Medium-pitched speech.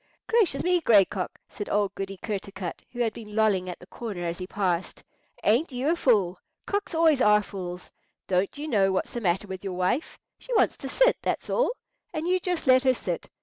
No: high, 210 Hz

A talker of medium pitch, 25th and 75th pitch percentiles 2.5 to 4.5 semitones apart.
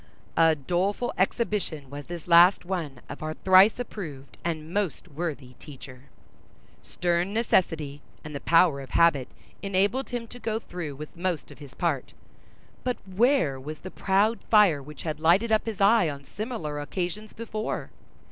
No: medium, 175 Hz; wide, 5.6 semitones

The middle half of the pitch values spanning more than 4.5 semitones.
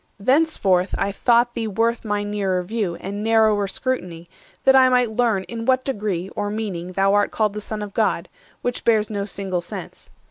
No: average, 3.0 semitones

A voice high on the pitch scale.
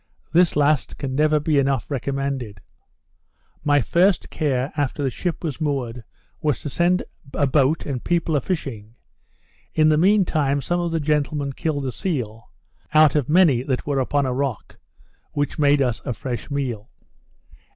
No: medium, 145 Hz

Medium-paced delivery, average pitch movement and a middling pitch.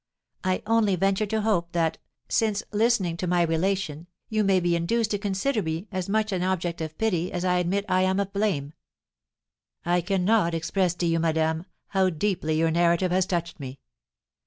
Yes: average, 180 wpm; average, 3.1 semitones; medium, 180 Hz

